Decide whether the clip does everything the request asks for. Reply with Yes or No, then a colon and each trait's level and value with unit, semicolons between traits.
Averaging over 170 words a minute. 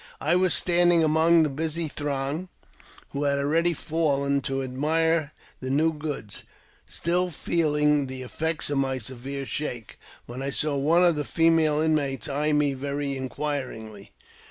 No: average, 150 wpm